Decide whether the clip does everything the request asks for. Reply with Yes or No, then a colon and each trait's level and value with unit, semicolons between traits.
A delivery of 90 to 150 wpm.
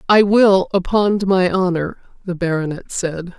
Yes: average, 140 wpm